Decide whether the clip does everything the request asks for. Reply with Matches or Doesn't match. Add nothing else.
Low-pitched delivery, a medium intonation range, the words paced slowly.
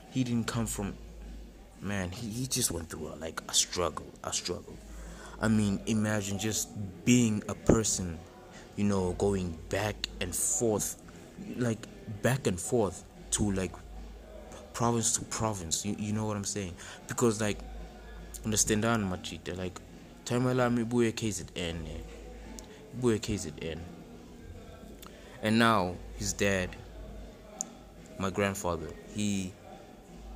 Matches